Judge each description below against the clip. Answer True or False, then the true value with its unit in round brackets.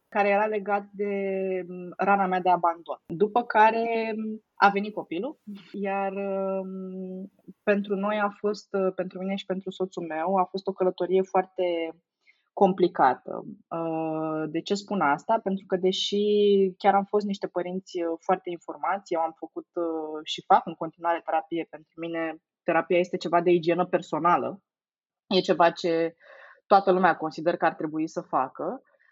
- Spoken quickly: False (145 wpm)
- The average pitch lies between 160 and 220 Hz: True (185 Hz)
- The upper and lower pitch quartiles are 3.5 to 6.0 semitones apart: False (2.8 semitones)